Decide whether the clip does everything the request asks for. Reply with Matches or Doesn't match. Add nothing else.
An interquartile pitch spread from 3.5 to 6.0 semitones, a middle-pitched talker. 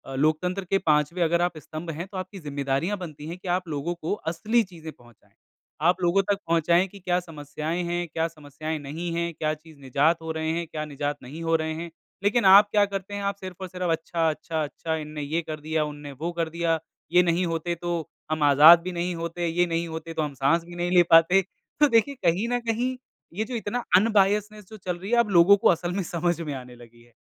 Doesn't match